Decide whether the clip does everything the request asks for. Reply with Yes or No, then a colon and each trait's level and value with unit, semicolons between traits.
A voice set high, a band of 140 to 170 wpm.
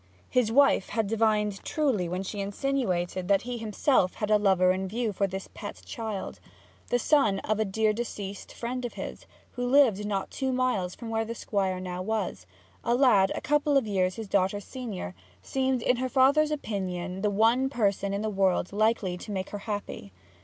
No: high, 210 Hz; average, 190 wpm